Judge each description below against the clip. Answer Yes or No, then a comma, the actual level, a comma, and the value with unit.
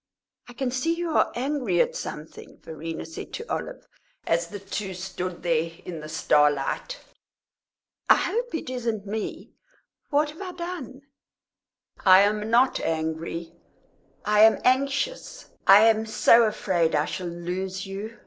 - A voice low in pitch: No, high, 210 Hz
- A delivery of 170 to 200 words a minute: No, average, 145 wpm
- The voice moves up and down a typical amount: No, wide, 7.4 semitones